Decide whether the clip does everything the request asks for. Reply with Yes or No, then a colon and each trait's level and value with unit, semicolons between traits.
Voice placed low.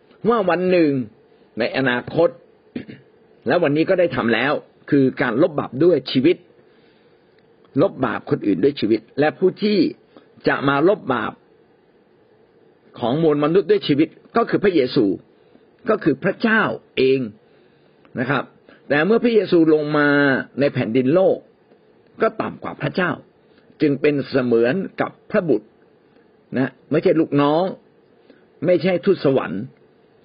No: medium, 160 Hz